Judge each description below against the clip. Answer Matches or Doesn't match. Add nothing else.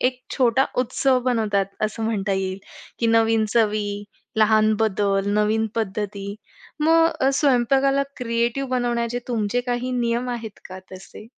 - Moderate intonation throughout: Matches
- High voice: Matches